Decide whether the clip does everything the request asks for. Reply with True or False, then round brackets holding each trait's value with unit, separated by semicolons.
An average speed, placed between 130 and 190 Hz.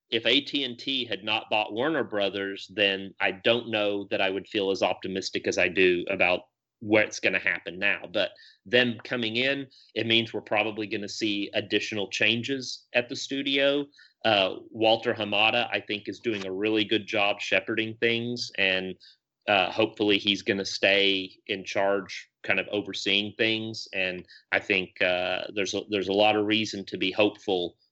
False (170 wpm; 110 Hz)